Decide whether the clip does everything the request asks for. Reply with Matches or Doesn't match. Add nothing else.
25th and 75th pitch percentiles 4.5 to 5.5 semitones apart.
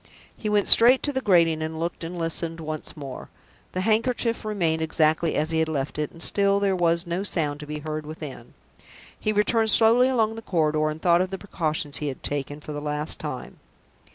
Matches